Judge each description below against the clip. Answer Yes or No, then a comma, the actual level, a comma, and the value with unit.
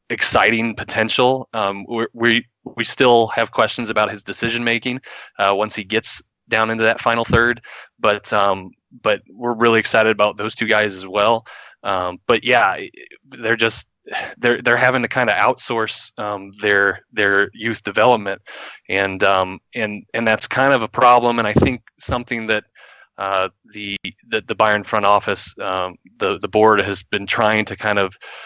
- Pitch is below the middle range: Yes, low, 110 Hz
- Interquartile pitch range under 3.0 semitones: Yes, narrow, 2.6 semitones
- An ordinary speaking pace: Yes, average, 170 wpm